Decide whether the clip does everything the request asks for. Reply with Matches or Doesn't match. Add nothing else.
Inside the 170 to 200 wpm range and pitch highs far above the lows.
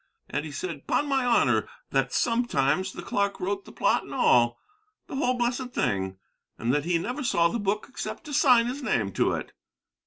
Matches